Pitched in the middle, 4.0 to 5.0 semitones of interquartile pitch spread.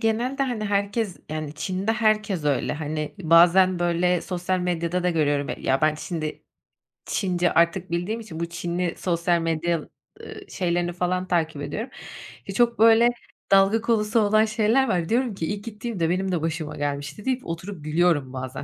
Yes: medium, 180 Hz; average, 4.4 semitones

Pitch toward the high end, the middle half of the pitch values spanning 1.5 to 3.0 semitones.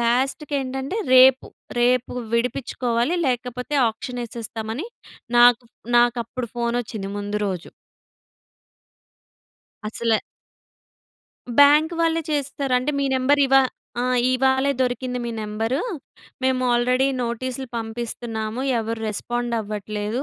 Yes: high, 245 Hz; narrow, 2.5 semitones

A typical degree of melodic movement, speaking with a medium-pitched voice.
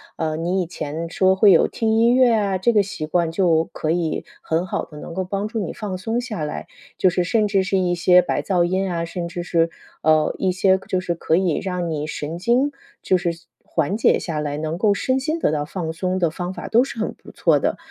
Yes: average, 3.3 semitones; medium, 180 Hz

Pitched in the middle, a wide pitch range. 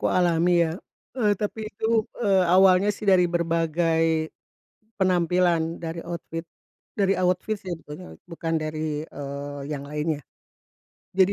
No: medium, 170 Hz; narrow, 2.5 semitones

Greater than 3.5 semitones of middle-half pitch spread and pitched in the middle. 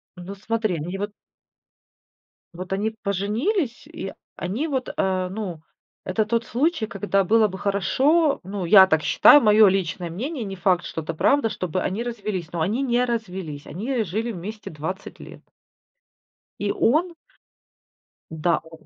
No: average, 4.2 semitones; high, 200 Hz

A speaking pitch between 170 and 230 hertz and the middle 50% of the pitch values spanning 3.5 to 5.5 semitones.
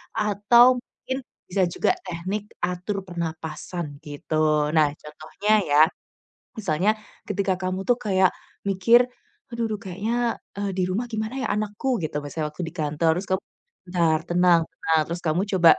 Yes: medium, 185 Hz; average, 4.5 semitones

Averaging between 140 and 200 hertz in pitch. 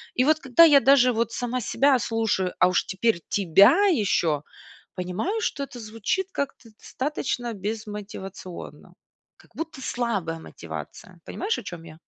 No: high, 230 Hz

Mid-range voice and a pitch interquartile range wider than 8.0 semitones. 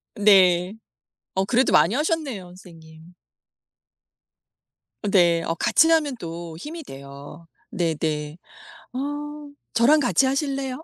No: high, 195 Hz; wide, 8.8 semitones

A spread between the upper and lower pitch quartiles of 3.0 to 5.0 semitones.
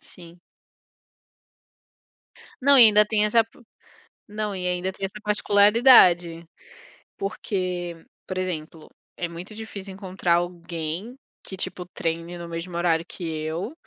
Yes: average, 3.6 semitones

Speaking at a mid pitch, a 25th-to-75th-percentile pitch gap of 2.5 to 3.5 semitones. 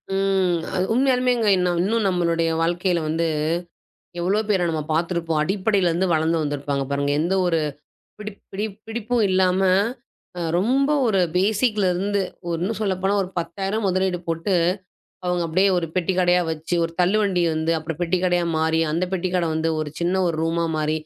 Yes: medium, 180 Hz; average, 2.9 semitones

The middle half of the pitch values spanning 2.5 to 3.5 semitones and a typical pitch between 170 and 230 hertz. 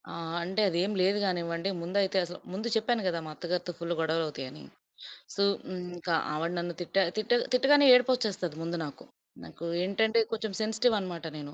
No: average, 4.3 semitones; medium, 185 Hz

